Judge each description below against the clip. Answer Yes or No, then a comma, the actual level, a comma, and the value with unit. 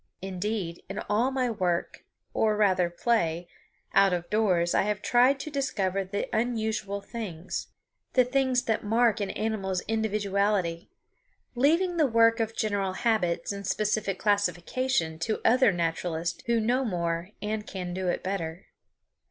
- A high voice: Yes, high, 205 Hz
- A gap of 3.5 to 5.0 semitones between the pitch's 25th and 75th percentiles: Yes, average, 4.0 semitones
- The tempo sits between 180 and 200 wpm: No, average, 145 wpm